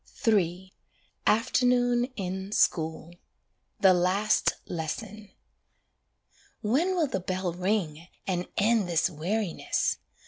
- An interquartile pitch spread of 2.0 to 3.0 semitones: No, average, 3.8 semitones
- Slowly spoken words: Yes, slow, 95 wpm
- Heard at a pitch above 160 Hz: Yes, high, 190 Hz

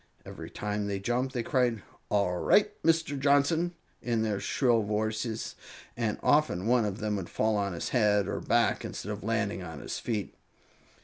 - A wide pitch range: No, average, 3.5 semitones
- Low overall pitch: Yes, low, 110 Hz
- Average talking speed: Yes, average, 175 wpm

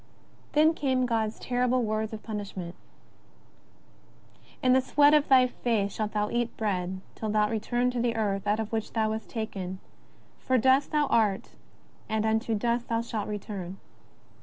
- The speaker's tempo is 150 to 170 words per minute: Yes, average, 165 wpm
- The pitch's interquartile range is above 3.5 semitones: No, average, 2.9 semitones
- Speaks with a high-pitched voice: Yes, high, 220 Hz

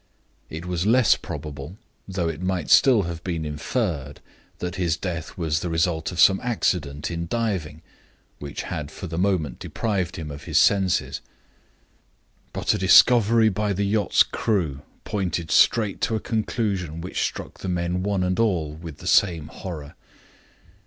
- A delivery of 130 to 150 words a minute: No, average, 160 wpm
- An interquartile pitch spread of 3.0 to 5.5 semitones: Yes, average, 3.9 semitones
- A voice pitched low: Yes, very low, 90 Hz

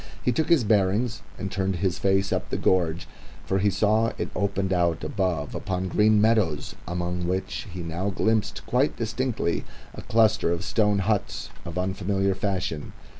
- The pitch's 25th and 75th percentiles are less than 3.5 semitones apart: Yes, average, 3.1 semitones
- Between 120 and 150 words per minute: No, average, 165 wpm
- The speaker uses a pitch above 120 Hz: No, very low, 95 Hz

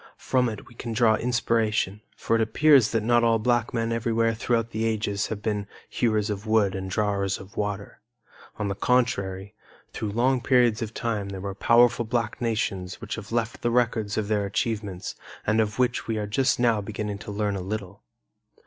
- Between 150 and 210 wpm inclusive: Yes, average, 195 wpm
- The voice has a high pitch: No, low, 110 Hz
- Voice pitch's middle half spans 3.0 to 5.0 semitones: No, narrow, 2.4 semitones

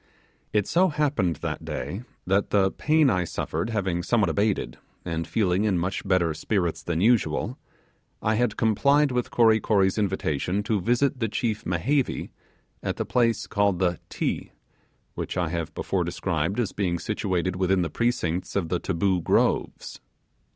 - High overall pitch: No, low, 100 Hz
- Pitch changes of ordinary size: Yes, average, 4.3 semitones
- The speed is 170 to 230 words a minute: No, average, 160 wpm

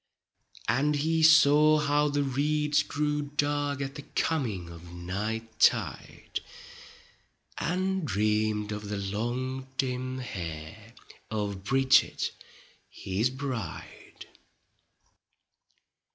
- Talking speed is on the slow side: Yes, slow, 95 wpm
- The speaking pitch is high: No, low, 130 Hz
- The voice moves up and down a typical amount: No, wide, 5.7 semitones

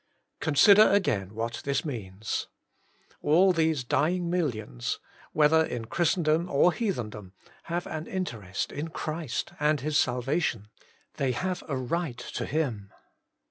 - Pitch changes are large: Yes, wide, 6.2 semitones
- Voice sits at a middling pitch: Yes, medium, 150 Hz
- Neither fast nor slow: No, slow, 130 wpm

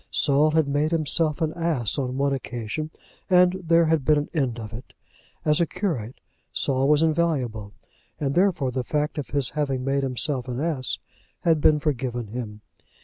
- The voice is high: No, medium, 145 Hz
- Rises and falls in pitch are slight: No, average, 3.7 semitones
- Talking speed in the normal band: Yes, average, 175 wpm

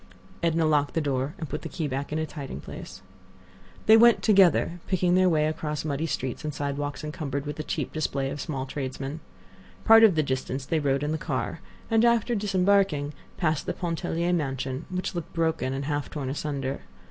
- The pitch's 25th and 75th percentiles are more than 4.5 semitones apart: No, average, 3.7 semitones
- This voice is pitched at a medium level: Yes, medium, 150 Hz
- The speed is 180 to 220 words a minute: Yes, average, 195 wpm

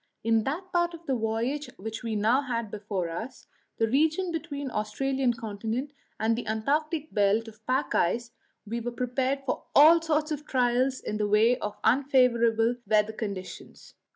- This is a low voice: No, high, 240 Hz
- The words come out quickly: No, average, 170 wpm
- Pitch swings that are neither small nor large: Yes, average, 4.3 semitones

